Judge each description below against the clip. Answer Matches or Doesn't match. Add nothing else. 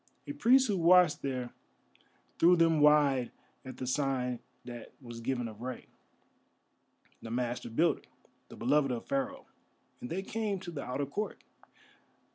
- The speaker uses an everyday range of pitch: Doesn't match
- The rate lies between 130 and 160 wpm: Matches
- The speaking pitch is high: Doesn't match